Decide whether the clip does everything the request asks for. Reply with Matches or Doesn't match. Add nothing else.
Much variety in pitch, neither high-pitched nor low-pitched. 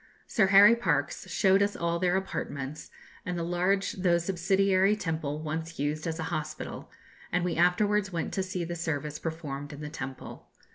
Doesn't match